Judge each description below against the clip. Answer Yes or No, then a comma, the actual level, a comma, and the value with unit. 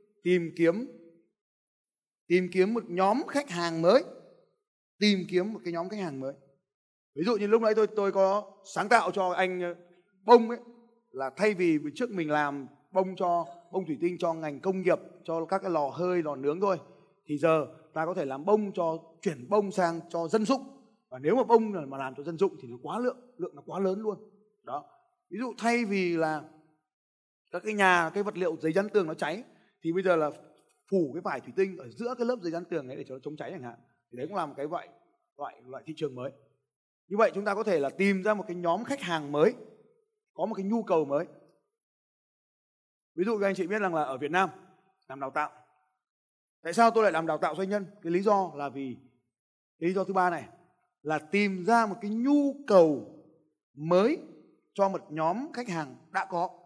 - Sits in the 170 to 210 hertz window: Yes, medium, 185 Hz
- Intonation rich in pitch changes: No, average, 4.6 semitones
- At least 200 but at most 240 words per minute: Yes, average, 220 wpm